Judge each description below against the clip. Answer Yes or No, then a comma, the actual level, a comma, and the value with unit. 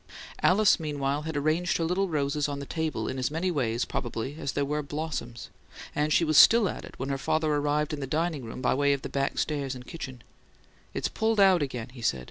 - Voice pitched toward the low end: No, medium, 145 Hz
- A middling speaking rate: No, fast, 235 wpm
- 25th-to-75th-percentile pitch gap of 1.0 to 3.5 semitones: Yes, average, 2.9 semitones